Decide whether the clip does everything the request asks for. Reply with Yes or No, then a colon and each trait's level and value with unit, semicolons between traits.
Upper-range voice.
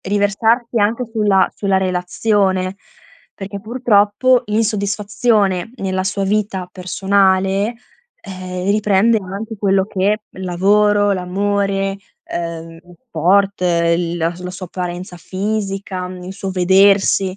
Yes: high, 195 Hz